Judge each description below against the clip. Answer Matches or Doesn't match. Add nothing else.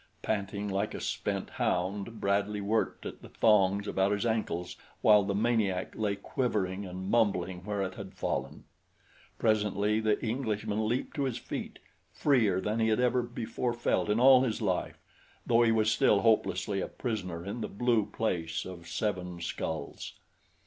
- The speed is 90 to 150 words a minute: Doesn't match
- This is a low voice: Matches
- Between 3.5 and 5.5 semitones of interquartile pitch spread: Doesn't match